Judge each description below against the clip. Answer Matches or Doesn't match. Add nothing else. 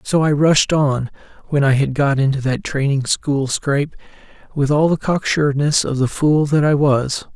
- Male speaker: Matches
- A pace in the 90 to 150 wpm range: Doesn't match